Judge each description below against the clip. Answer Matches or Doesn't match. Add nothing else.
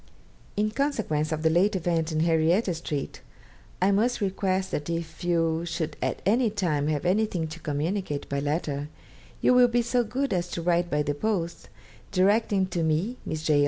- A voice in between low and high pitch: Matches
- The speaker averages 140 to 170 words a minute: Doesn't match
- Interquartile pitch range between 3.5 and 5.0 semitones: Matches